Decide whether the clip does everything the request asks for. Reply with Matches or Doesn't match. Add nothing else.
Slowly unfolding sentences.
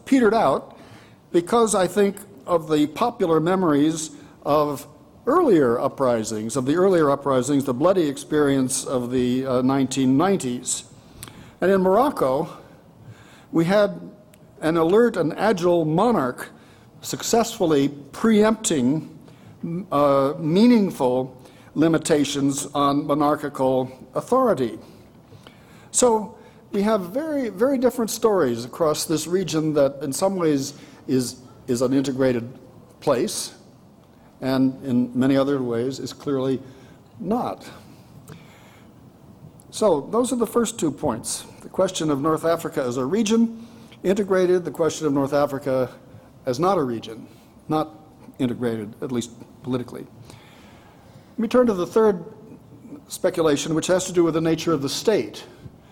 Matches